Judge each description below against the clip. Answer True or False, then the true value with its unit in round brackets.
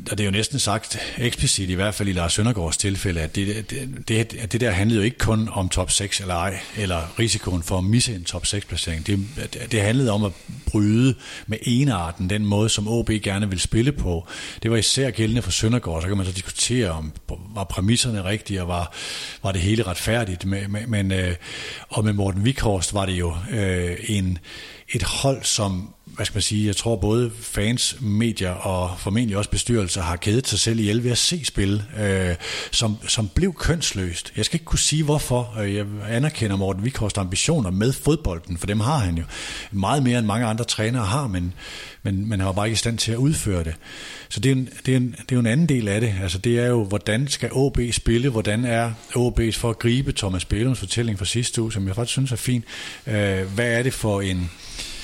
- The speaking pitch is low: True (105 Hz)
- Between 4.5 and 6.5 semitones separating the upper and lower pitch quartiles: False (3.6 semitones)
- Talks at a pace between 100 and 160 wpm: False (220 wpm)